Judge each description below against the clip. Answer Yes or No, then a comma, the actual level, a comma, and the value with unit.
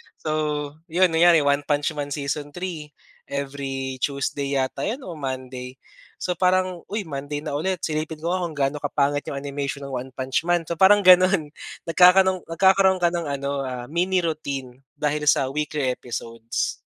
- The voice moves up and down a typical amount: Yes, average, 3.9 semitones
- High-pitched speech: No, medium, 150 Hz